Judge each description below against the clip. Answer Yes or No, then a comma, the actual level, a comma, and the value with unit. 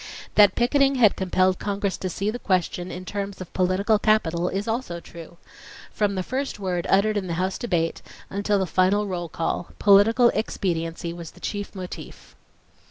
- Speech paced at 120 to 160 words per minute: No, average, 170 wpm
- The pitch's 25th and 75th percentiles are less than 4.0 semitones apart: Yes, average, 2.8 semitones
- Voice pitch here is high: Yes, high, 195 Hz